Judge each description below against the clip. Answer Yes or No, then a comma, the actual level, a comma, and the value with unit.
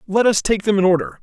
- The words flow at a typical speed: No, fast, 295 wpm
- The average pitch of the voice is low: No, high, 195 Hz